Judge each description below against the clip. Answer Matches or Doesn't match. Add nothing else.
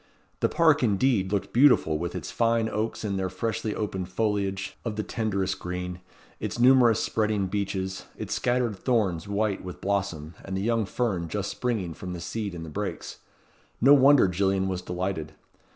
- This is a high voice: Doesn't match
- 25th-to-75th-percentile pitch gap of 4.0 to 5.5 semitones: Doesn't match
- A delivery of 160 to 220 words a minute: Matches